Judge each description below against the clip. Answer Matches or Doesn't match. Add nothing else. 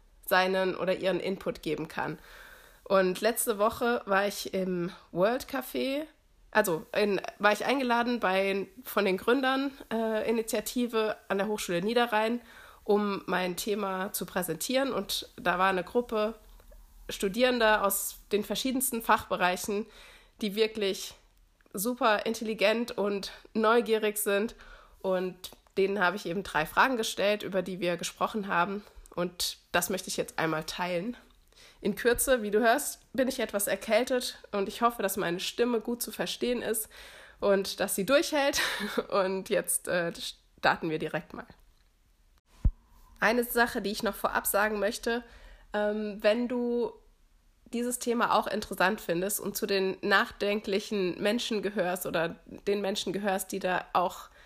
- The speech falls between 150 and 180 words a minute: Doesn't match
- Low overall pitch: Doesn't match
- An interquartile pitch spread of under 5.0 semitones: Matches